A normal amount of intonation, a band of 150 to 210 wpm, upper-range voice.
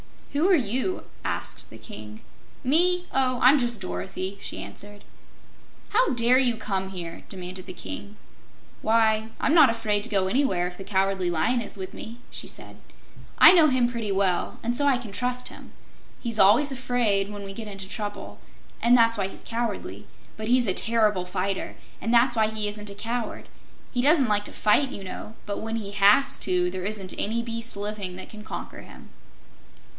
Yes: average, 3.8 semitones; average, 190 wpm; high, 215 Hz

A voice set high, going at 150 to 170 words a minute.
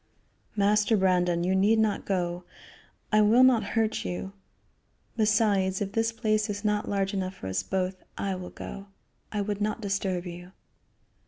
Yes: high, 200 Hz; average, 160 wpm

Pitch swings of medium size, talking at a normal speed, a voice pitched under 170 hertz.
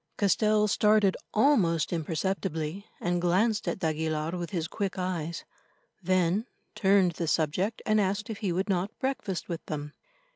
No: average, 3.7 semitones; average, 145 wpm; medium, 185 Hz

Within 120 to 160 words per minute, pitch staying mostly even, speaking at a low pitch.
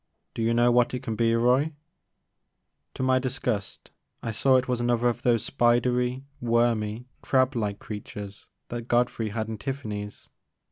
Yes: average, 150 wpm; narrow, 2.1 semitones; low, 120 Hz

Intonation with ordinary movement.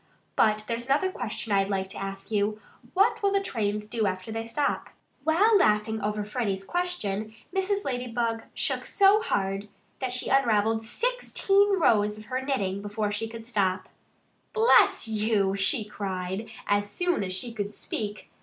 Yes: average, 4.6 semitones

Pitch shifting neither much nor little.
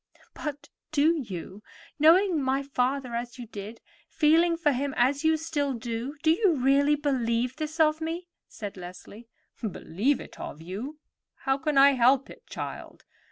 Yes: average, 4.5 semitones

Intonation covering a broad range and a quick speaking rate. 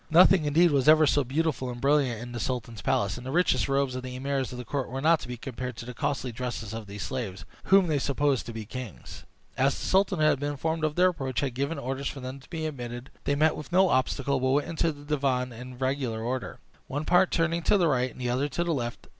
No: average, 3.5 semitones; fast, 265 wpm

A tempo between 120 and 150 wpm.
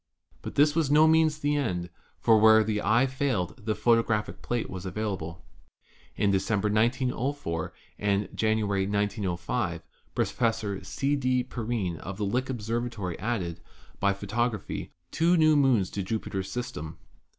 Yes: average, 140 wpm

